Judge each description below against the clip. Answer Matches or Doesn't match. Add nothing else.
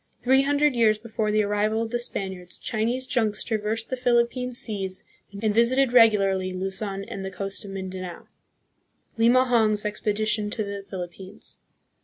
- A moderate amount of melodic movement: Matches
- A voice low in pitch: Doesn't match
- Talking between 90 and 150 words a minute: Matches